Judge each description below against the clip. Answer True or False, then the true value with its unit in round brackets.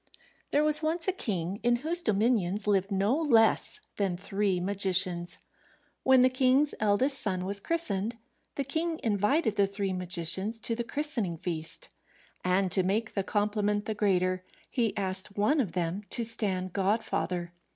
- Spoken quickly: False (155 wpm)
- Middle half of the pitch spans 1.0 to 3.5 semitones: False (4.4 semitones)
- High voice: True (205 Hz)